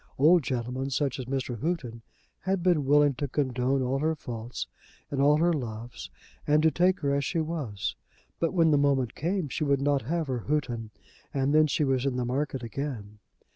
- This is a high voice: No, medium, 140 Hz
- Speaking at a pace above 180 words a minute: Yes, average, 200 wpm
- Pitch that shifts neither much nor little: Yes, average, 3.6 semitones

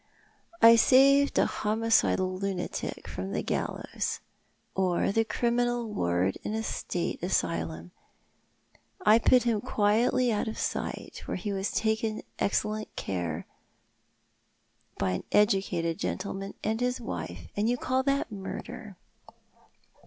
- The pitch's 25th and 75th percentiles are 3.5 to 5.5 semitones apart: Yes, average, 4.4 semitones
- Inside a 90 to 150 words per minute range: Yes, average, 140 wpm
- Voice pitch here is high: Yes, high, 210 Hz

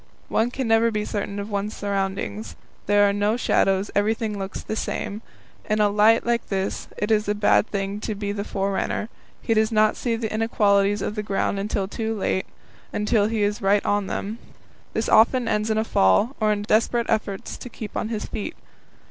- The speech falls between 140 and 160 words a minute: No, average, 200 wpm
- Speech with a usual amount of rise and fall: No, narrow, 1.7 semitones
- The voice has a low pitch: No, high, 210 Hz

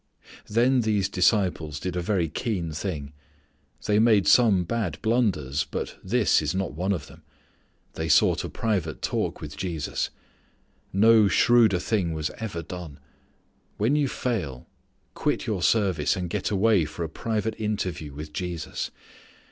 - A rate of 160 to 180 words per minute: No, average, 150 wpm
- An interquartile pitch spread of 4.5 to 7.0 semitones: Yes, wide, 5.6 semitones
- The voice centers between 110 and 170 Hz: No, very low, 95 Hz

